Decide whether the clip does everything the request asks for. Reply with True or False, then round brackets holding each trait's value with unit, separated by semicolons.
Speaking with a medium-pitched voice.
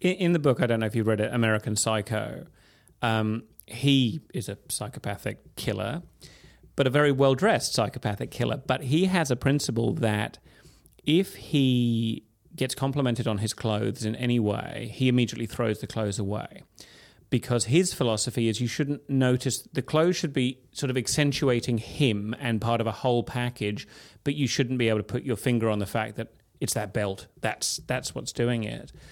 False (120 Hz)